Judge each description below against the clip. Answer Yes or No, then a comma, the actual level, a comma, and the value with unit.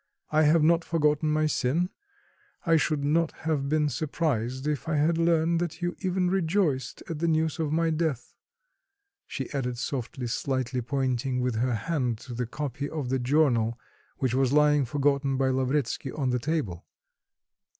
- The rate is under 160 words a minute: No, average, 165 wpm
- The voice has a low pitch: No, medium, 145 Hz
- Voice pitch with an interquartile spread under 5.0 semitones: Yes, average, 3.7 semitones